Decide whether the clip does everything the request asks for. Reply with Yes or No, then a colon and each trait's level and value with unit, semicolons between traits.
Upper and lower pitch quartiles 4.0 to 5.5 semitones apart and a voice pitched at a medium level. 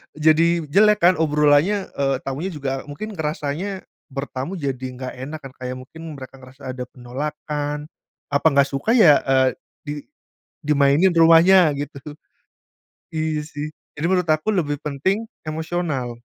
No: average, 3.3 semitones; medium, 150 Hz